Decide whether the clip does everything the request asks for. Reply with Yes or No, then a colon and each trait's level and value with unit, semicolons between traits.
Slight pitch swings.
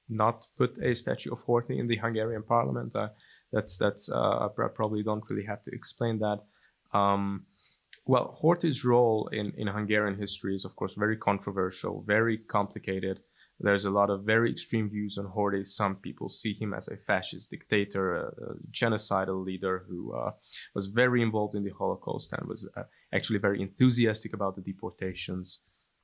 Yes: narrow, 2.2 semitones